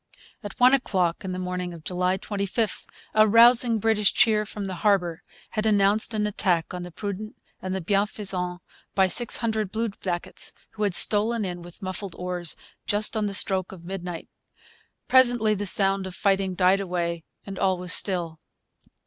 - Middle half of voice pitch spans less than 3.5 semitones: Yes, average, 2.8 semitones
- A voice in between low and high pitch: No, high, 195 Hz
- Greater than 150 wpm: Yes, average, 170 wpm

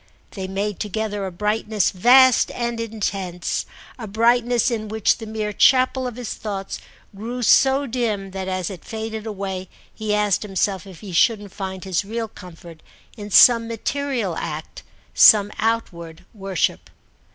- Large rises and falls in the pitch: No, average, 3.1 semitones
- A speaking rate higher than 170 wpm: No, average, 150 wpm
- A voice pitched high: Yes, high, 210 Hz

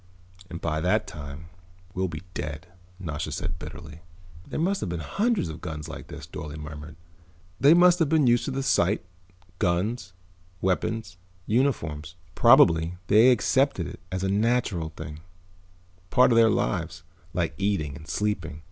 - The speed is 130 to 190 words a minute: Yes, average, 155 wpm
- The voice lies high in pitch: No, very low, 90 Hz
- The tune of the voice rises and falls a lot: Yes, wide, 6.6 semitones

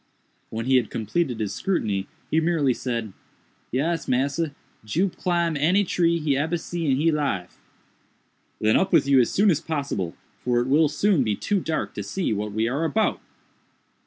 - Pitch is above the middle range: No, medium, 145 Hz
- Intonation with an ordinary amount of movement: No, wide, 6.3 semitones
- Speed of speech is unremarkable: Yes, average, 180 wpm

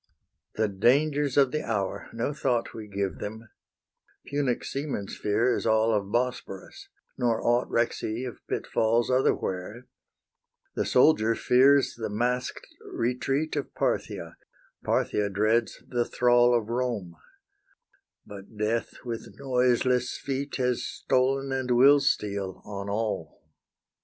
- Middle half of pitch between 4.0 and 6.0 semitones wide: No, average, 3.3 semitones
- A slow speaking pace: Yes, slow, 125 wpm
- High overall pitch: No, low, 120 Hz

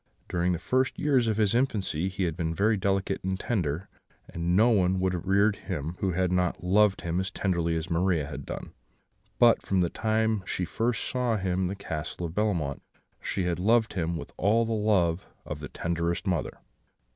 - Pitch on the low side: Yes, very low, 95 Hz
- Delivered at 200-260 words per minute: Yes, fast, 205 wpm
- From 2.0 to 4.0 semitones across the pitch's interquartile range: Yes, average, 3.7 semitones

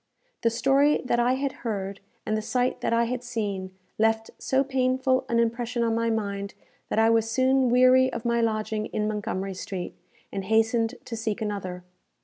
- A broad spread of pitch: No, average, 2.8 semitones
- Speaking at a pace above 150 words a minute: Yes, average, 180 wpm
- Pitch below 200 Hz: No, high, 230 Hz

